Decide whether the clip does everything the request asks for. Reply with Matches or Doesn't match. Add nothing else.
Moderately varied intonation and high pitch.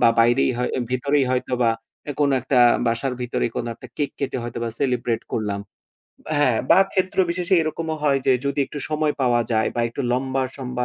Doesn't match